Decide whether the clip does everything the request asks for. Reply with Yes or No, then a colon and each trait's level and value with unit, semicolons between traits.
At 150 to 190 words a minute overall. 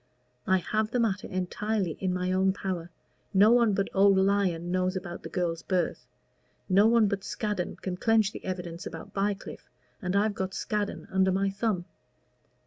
Yes: average, 170 wpm